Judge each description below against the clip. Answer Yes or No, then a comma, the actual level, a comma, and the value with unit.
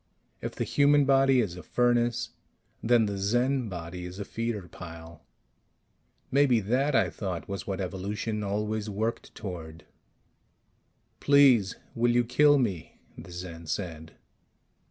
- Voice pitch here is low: Yes, low, 105 Hz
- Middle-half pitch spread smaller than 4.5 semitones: No, average, 5.3 semitones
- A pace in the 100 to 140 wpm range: Yes, slow, 135 wpm